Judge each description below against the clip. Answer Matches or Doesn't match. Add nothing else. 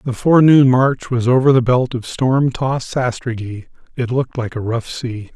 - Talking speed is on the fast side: Doesn't match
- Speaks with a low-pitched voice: Matches